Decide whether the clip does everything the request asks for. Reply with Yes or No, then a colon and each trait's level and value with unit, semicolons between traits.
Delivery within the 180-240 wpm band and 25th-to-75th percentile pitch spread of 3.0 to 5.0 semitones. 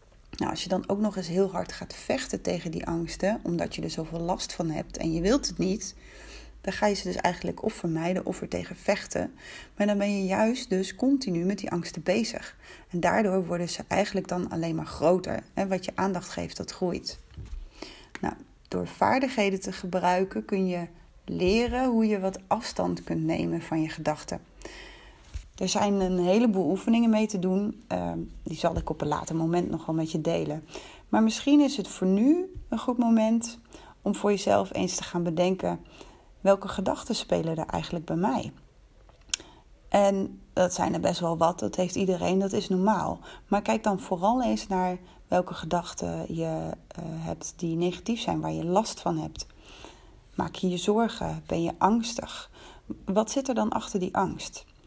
Yes: average, 185 wpm; average, 3.8 semitones